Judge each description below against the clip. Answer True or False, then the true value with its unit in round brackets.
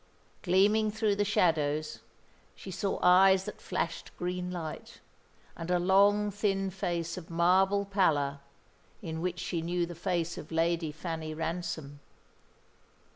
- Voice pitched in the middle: True (175 Hz)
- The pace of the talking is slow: True (130 wpm)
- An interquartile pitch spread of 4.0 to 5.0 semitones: False (2.8 semitones)